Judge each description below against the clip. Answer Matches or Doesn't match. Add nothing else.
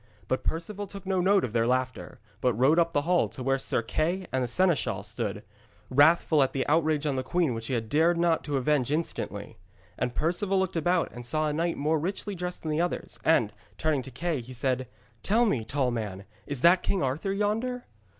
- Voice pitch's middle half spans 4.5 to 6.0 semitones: Matches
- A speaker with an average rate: Doesn't match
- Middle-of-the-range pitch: Matches